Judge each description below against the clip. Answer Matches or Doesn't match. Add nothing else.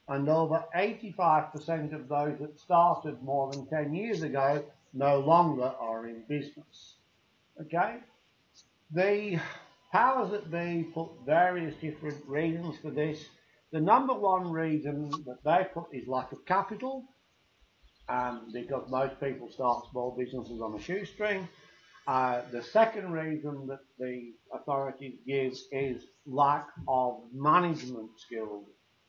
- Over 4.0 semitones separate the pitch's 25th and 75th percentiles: Matches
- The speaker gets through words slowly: Matches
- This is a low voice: Doesn't match